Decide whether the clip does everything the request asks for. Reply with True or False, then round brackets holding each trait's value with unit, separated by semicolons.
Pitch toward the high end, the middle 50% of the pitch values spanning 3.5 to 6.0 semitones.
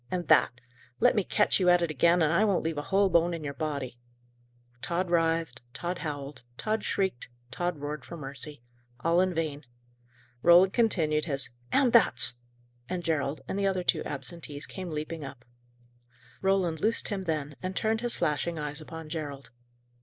False (165 Hz; 3.8 semitones)